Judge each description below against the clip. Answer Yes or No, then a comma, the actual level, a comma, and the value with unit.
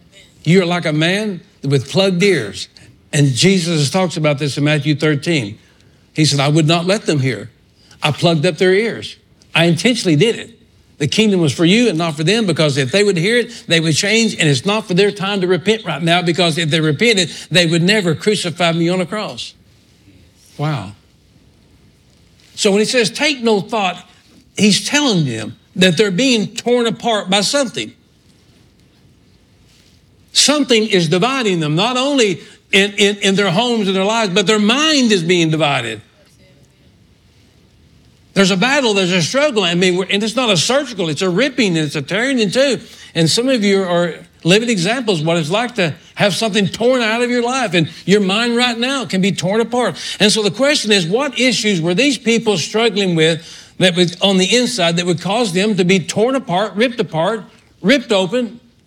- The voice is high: Yes, high, 195 Hz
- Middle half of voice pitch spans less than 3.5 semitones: No, average, 4.9 semitones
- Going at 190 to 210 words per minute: Yes, average, 195 wpm